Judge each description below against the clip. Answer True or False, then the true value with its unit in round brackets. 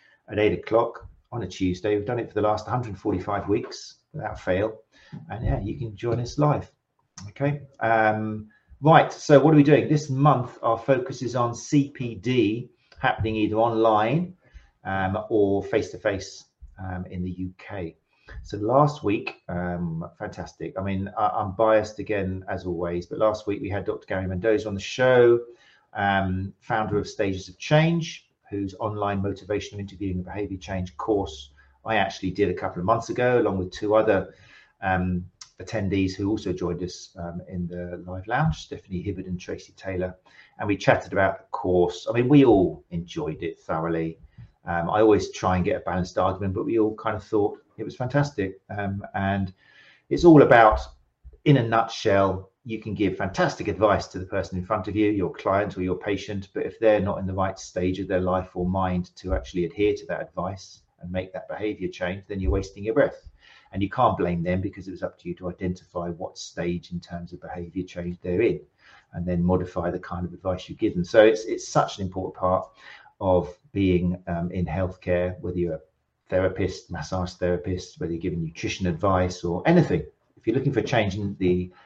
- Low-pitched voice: True (95 Hz)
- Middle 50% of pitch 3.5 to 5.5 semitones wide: False (3.1 semitones)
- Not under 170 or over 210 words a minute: True (195 wpm)